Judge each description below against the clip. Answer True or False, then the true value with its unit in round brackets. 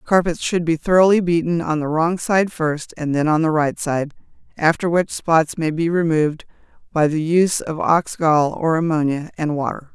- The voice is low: False (160 Hz)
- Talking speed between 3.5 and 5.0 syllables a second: True (4.8 syllables/s)